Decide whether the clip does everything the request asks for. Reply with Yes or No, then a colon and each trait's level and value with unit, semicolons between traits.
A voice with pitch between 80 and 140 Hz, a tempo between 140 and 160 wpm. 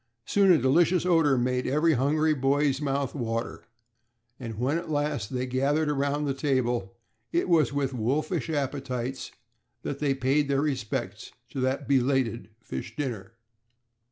Yes: low, 135 Hz; average, 145 wpm